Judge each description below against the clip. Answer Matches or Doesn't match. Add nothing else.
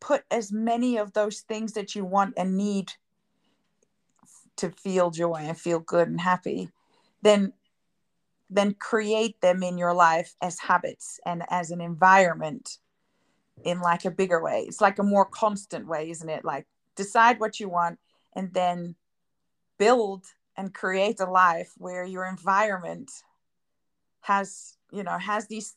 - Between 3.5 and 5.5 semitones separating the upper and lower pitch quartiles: Doesn't match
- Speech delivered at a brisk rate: Doesn't match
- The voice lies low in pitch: Doesn't match